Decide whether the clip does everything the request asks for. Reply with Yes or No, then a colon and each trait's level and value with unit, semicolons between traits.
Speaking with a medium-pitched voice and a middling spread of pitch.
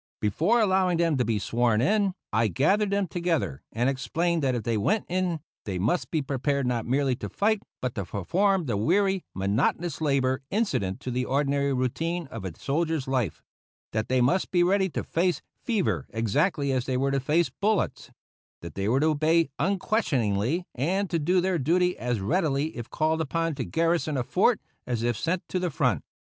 No: medium, 145 Hz; wide, 6.3 semitones